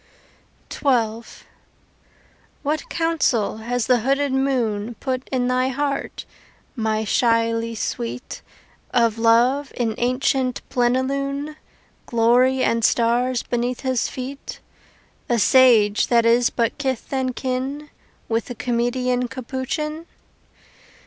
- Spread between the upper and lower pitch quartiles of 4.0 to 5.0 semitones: No, narrow, 2.4 semitones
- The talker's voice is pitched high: Yes, very high, 250 Hz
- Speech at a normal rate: No, slow, 105 wpm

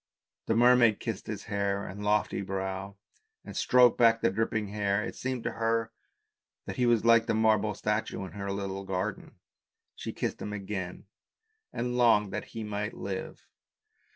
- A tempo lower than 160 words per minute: No, average, 165 wpm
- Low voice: Yes, low, 105 Hz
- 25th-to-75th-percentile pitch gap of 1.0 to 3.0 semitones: Yes, narrow, 2.5 semitones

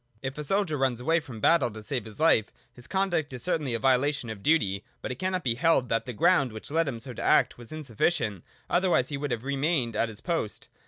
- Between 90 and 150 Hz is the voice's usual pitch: Yes, low, 135 Hz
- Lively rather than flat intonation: Yes, wide, 5.7 semitones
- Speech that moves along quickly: Yes, fast, 245 wpm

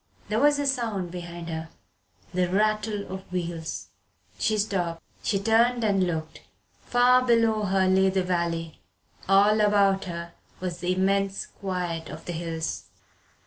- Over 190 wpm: No, average, 145 wpm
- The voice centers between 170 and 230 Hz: Yes, high, 190 Hz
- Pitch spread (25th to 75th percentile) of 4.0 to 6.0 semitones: No, average, 3.6 semitones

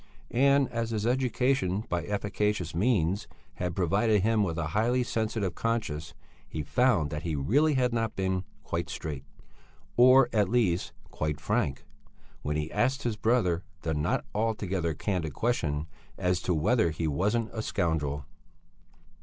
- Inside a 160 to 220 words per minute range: No, average, 145 wpm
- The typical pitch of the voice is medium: No, low, 100 Hz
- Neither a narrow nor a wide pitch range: No, wide, 6.1 semitones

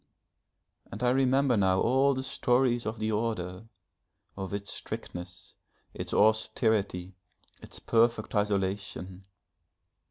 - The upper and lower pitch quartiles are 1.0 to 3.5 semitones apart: No, average, 3.9 semitones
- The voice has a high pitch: No, low, 110 Hz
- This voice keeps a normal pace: No, slow, 105 wpm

